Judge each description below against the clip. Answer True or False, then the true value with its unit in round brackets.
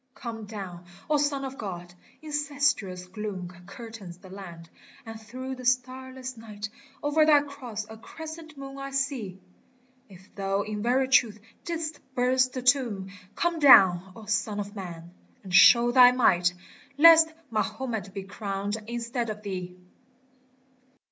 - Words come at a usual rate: True (145 wpm)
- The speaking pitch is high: True (225 Hz)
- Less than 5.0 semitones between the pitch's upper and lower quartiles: False (5.3 semitones)